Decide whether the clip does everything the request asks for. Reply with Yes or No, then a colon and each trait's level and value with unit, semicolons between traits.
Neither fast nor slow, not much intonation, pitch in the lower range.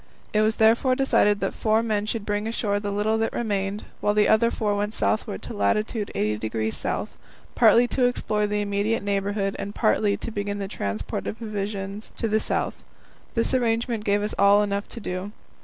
No: average, 190 wpm; narrow, 1.6 semitones; high, 210 Hz